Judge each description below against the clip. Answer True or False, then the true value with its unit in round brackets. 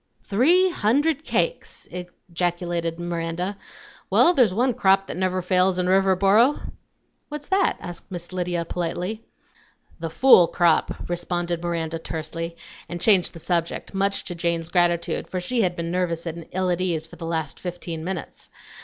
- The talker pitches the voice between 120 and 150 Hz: False (175 Hz)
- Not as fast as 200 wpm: True (155 wpm)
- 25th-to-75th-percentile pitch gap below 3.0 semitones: True (2.4 semitones)